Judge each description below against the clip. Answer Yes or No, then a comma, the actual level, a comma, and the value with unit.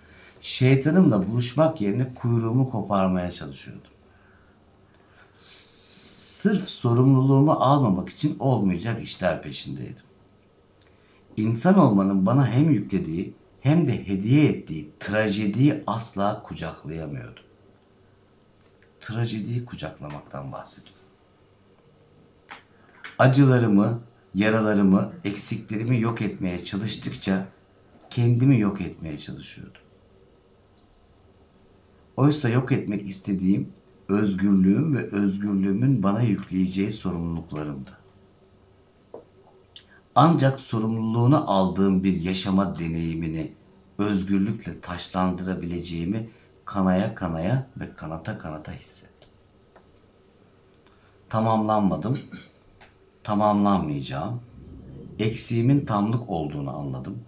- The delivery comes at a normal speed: No, slow, 70 wpm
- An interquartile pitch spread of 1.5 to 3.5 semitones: Yes, average, 3.1 semitones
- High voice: No, low, 100 Hz